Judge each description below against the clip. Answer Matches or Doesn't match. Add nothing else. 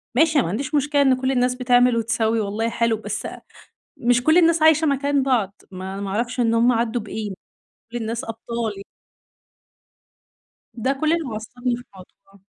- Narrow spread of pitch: Doesn't match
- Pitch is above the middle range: Matches